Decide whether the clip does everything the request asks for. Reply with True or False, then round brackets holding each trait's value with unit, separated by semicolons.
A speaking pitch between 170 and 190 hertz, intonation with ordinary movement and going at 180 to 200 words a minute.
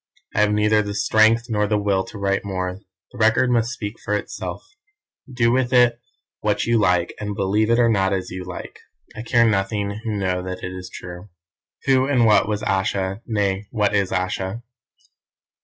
False (105 Hz; 3.0 semitones; 190 wpm)